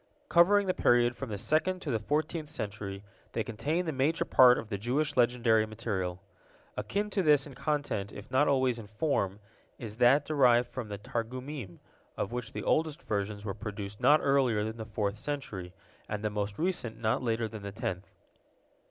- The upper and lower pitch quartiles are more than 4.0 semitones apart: Yes, wide, 5.5 semitones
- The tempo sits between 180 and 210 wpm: Yes, average, 185 wpm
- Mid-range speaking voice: No, low, 120 Hz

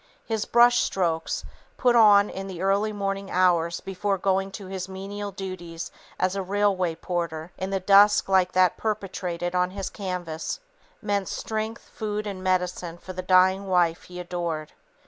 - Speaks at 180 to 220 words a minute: No, average, 160 wpm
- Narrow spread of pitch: Yes, narrow, 2.1 semitones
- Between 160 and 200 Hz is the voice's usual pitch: Yes, high, 190 Hz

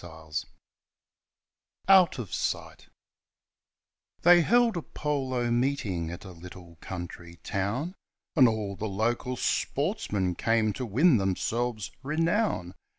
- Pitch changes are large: Yes, wide, 7.7 semitones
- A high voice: No, low, 115 Hz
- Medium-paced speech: No, slow, 110 wpm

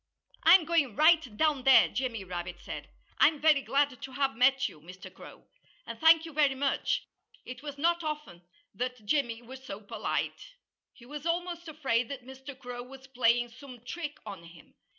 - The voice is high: Yes, very high, 270 Hz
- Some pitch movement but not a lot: Yes, average, 4.0 semitones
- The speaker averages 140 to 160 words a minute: No, average, 175 wpm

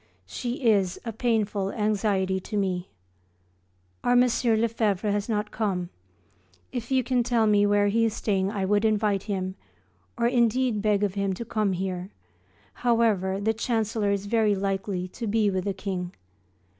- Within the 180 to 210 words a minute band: No, average, 160 wpm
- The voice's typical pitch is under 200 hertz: No, high, 205 Hz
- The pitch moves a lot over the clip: No, average, 2.7 semitones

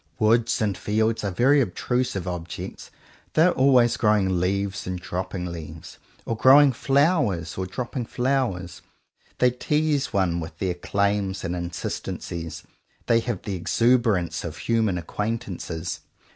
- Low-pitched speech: Yes, low, 105 Hz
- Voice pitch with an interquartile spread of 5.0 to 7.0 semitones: Yes, wide, 5.5 semitones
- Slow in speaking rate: Yes, slow, 130 wpm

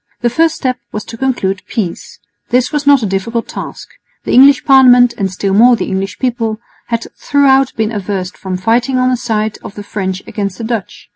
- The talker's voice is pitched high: Yes, high, 230 Hz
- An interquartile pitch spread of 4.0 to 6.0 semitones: Yes, average, 4.3 semitones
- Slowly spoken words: No, average, 200 wpm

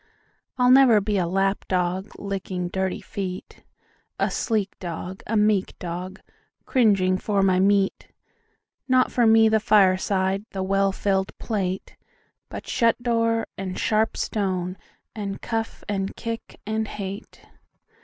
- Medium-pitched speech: No, high, 195 Hz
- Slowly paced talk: Yes, slow, 125 wpm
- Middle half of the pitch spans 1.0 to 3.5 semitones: Yes, narrow, 2.6 semitones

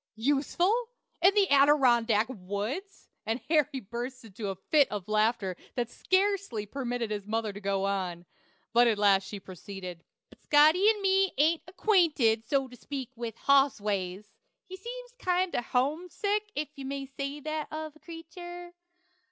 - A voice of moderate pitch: No, very high, 270 Hz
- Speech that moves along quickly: No, average, 160 wpm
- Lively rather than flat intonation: Yes, wide, 7.9 semitones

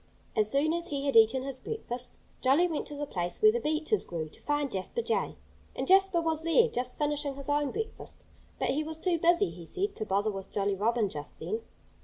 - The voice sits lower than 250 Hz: No, very high, 290 Hz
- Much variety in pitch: Yes, wide, 7.2 semitones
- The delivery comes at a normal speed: No, fast, 220 wpm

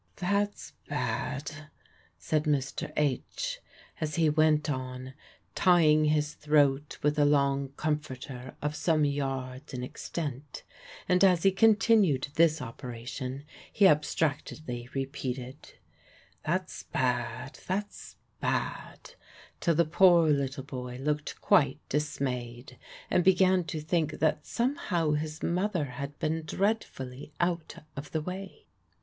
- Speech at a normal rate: No, slow, 120 wpm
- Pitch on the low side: No, medium, 150 Hz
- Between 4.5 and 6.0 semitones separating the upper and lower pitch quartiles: No, average, 3.9 semitones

